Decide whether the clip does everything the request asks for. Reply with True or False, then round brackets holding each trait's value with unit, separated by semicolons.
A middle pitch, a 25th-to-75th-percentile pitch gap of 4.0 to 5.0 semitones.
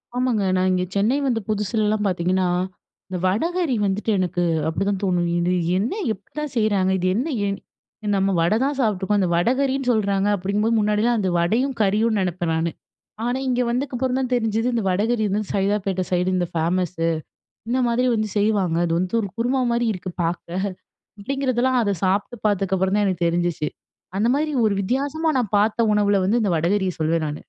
False (205 Hz; 4.5 semitones)